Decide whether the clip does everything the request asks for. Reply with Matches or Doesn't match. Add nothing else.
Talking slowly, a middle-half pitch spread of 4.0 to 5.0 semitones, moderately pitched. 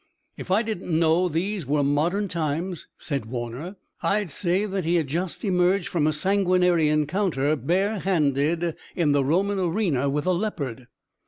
Doesn't match